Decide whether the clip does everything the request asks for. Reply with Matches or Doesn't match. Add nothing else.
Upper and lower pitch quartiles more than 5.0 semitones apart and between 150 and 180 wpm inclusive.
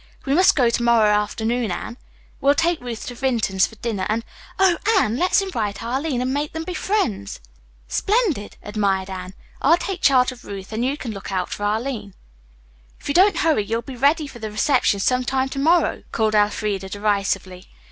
Doesn't match